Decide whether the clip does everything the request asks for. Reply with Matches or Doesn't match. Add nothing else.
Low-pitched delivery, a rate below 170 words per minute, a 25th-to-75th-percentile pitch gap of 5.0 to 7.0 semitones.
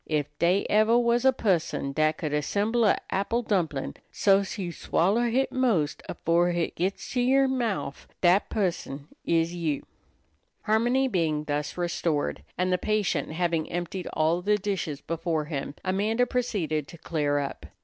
Doesn't match